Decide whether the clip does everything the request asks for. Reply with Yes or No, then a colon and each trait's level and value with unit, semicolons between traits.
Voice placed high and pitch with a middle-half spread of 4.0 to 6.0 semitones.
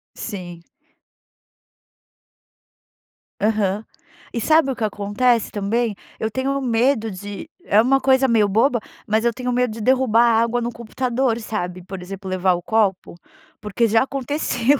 No: high, 225 Hz; average, 3.5 semitones